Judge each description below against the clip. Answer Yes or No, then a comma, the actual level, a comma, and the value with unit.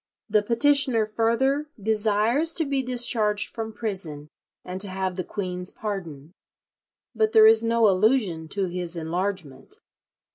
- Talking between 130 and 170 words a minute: Yes, slow, 135 wpm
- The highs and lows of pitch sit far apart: No, average, 4.0 semitones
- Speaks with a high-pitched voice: Yes, high, 210 Hz